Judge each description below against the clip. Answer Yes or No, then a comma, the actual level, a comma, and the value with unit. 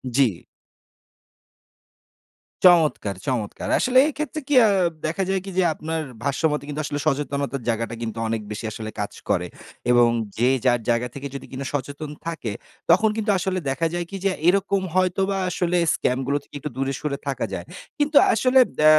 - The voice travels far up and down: Yes, wide, 6.7 semitones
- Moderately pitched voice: Yes, medium, 150 Hz